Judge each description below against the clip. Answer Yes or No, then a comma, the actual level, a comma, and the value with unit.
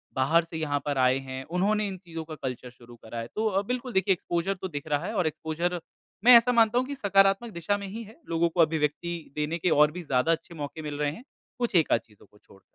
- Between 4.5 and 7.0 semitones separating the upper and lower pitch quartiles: Yes, average, 5.2 semitones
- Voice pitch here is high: No, medium, 165 Hz